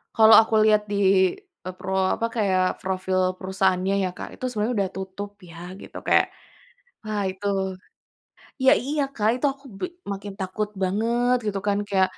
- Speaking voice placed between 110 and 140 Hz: No, high, 200 Hz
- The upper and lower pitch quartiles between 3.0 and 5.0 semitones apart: No, narrow, 2.6 semitones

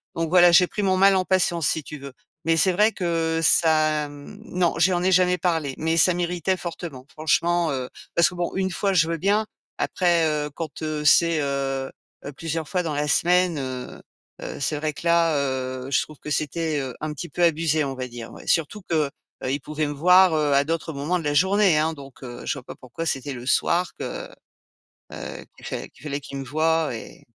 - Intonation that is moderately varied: Yes, average, 3.5 semitones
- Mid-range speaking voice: Yes, medium, 160 Hz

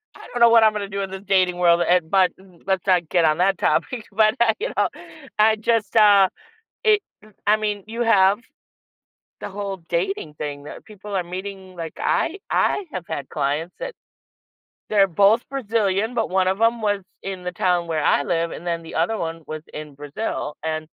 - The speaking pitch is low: No, high, 190 Hz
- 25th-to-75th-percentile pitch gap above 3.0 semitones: Yes, average, 4.0 semitones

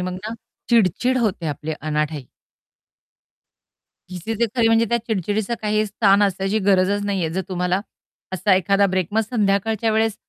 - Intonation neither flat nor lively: Yes, average, 3.1 semitones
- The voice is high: Yes, high, 200 Hz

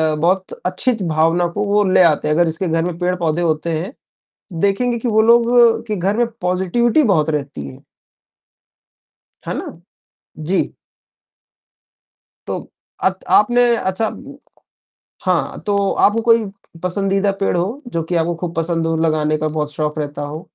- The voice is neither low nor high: Yes, medium, 180 Hz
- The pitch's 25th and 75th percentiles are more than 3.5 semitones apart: Yes, average, 4.1 semitones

